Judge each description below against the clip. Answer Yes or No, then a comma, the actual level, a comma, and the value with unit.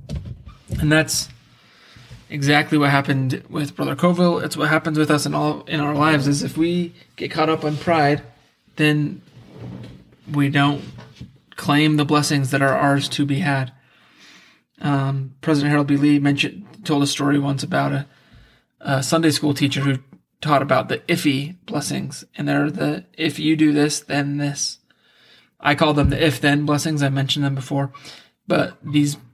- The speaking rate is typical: Yes, average, 165 wpm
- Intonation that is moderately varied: No, narrow, 1.6 semitones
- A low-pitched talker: No, medium, 145 Hz